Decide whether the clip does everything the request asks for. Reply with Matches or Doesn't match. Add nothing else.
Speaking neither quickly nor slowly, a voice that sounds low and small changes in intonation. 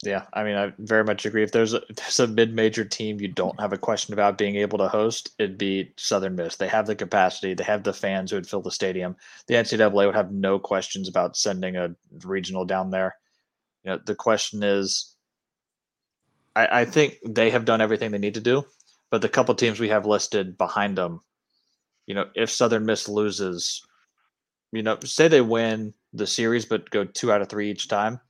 Doesn't match